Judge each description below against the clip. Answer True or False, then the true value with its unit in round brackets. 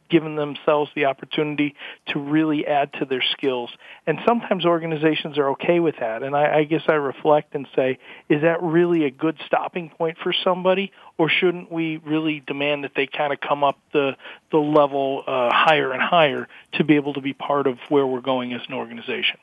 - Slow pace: False (200 wpm)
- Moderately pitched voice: True (150 Hz)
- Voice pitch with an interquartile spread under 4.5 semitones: True (2.8 semitones)